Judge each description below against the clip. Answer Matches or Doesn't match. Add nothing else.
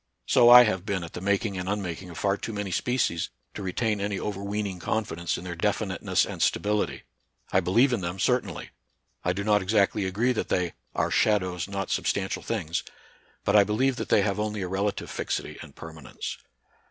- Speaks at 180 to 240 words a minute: Matches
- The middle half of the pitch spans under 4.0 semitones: Matches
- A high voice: Doesn't match